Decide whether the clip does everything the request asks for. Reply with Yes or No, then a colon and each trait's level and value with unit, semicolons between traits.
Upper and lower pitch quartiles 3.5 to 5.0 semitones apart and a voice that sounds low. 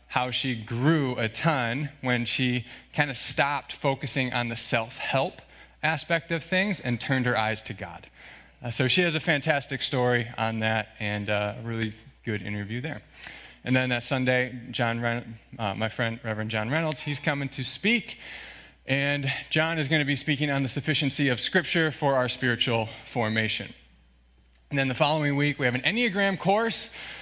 Yes: average, 4.4 semitones; low, 130 Hz